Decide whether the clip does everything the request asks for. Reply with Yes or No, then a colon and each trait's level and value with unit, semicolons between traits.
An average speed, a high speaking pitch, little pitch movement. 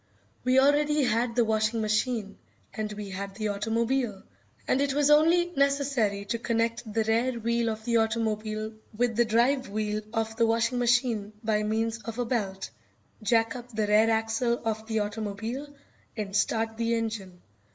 Yes: average, 165 wpm; high, 225 Hz; narrow, 2.1 semitones